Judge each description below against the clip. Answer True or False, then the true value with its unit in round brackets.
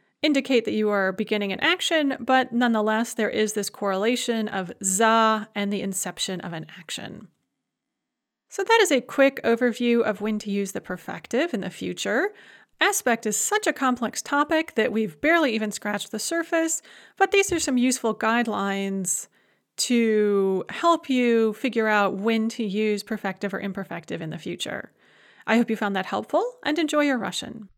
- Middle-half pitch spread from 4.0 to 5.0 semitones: True (4.7 semitones)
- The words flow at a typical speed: True (170 wpm)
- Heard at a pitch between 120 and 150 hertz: False (225 Hz)